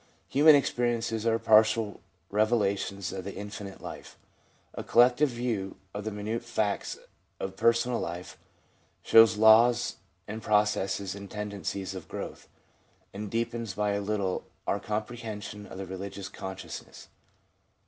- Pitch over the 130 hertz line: No, low, 105 Hz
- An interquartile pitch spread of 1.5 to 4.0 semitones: Yes, narrow, 2.5 semitones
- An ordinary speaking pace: No, slow, 130 wpm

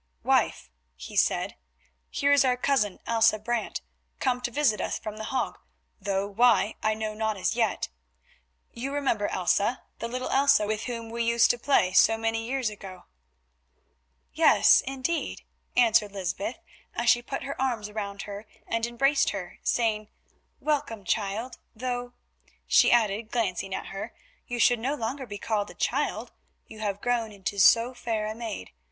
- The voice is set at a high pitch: Yes, high, 225 Hz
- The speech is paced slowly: No, average, 160 wpm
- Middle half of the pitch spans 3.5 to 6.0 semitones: No, average, 2.8 semitones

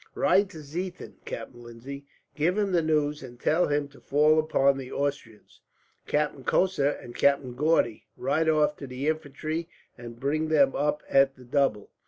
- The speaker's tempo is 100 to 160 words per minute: No, average, 170 wpm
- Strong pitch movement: No, average, 2.7 semitones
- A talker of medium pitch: Yes, medium, 145 Hz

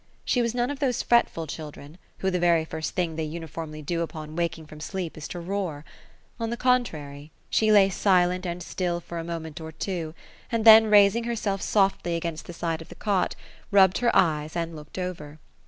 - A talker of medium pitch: Yes, medium, 175 Hz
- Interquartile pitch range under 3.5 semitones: No, average, 4.0 semitones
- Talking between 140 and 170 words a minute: No, fast, 205 wpm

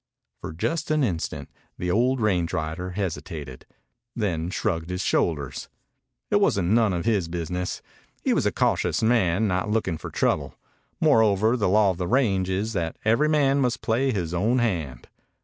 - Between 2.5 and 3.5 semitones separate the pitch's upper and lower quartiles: No, average, 4.8 semitones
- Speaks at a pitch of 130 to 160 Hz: No, very low, 95 Hz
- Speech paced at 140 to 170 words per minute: Yes, average, 165 wpm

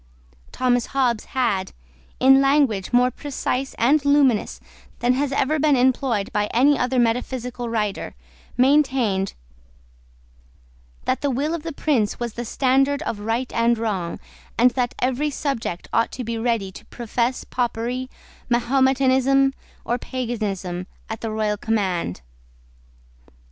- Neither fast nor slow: No, slow, 130 wpm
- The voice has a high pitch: Yes, high, 245 Hz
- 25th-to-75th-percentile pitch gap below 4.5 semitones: Yes, average, 3.2 semitones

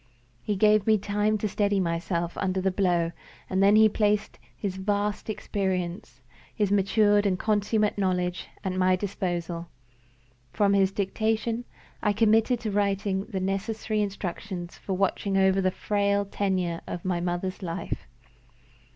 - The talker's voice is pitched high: Yes, high, 195 Hz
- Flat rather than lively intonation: Yes, narrow, 2.1 semitones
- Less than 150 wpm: Yes, average, 140 wpm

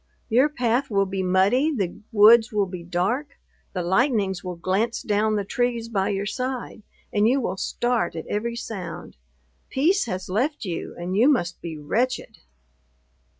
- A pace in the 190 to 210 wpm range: No, average, 160 wpm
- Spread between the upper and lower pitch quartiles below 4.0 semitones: No, average, 4.7 semitones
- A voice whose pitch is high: Yes, high, 210 Hz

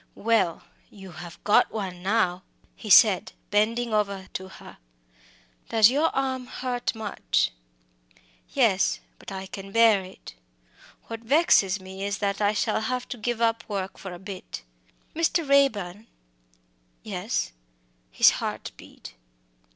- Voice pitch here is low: No, high, 210 Hz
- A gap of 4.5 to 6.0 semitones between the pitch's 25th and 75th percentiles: No, average, 3.4 semitones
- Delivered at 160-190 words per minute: No, slow, 135 wpm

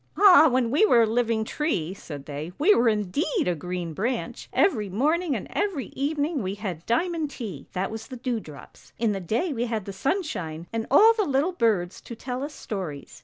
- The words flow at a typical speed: No, fast, 215 wpm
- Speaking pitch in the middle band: No, high, 230 Hz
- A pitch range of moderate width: No, wide, 7.5 semitones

